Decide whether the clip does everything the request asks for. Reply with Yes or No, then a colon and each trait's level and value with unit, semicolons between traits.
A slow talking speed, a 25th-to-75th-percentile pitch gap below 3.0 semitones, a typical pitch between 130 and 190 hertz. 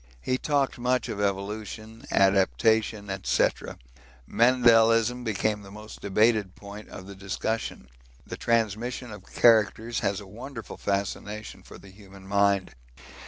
No: slow, 125 wpm; narrow, 2.5 semitones; low, 105 Hz